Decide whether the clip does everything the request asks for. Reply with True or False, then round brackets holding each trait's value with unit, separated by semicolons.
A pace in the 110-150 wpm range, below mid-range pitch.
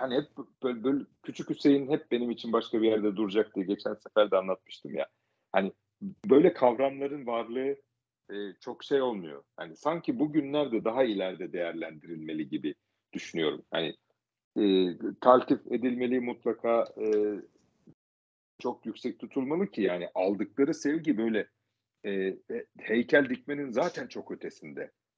True (135 wpm; 115 Hz)